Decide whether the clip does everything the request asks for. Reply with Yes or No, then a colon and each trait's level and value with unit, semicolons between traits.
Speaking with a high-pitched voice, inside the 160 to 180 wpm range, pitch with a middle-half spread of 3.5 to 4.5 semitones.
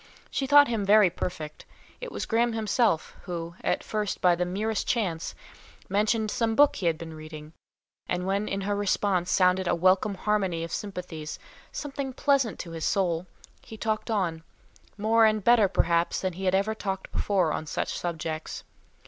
Yes: high, 195 Hz; average, 175 wpm; average, 4.1 semitones